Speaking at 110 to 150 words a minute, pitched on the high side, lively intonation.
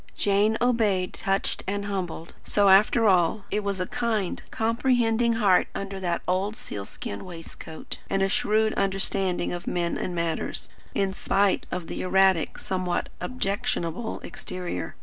No: average, 140 wpm; high, 195 Hz; average, 2.8 semitones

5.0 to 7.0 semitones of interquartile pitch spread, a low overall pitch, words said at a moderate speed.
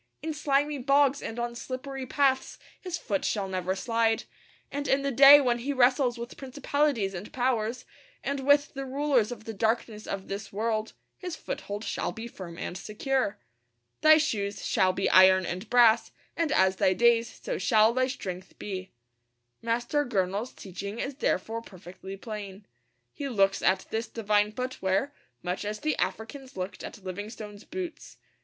No: average, 5.3 semitones; high, 230 Hz; average, 165 wpm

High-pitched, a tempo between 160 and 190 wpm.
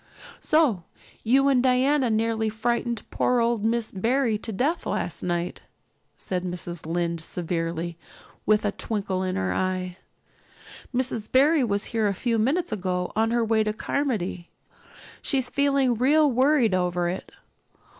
No: high, 220 Hz; average, 145 wpm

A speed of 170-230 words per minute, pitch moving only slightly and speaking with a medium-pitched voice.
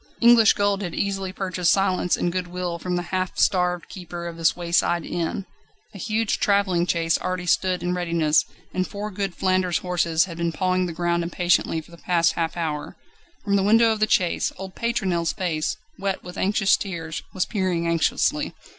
Yes: average, 185 wpm; narrow, 2.2 semitones; medium, 180 Hz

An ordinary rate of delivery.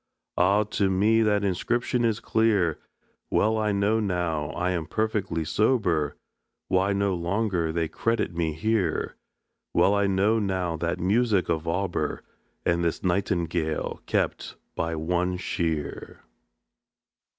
No: slow, 125 wpm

